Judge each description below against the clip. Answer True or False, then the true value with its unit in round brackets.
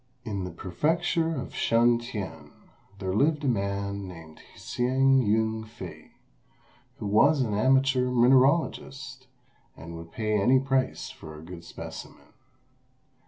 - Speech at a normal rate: False (125 wpm)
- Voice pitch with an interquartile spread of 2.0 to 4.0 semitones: False (5.2 semitones)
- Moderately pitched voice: False (120 Hz)